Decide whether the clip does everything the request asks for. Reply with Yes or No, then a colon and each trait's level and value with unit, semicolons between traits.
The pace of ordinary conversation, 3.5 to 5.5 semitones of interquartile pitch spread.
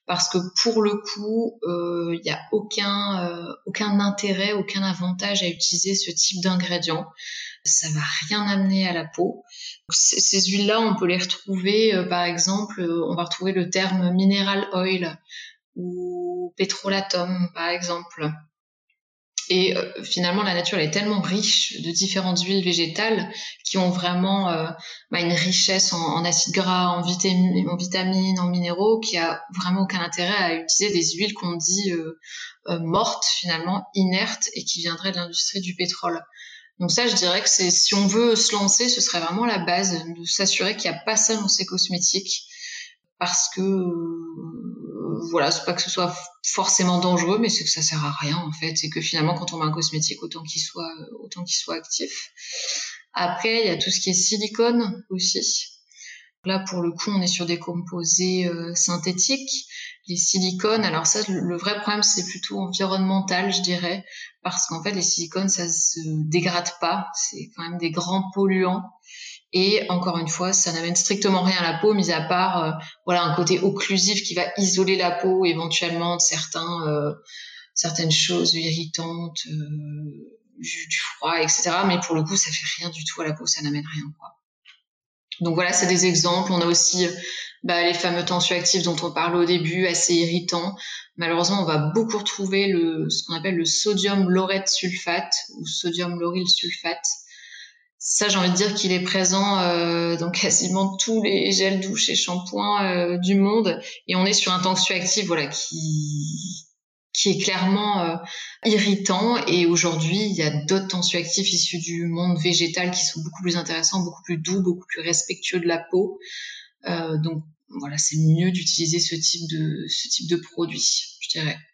No: average, 180 wpm; narrow, 2.4 semitones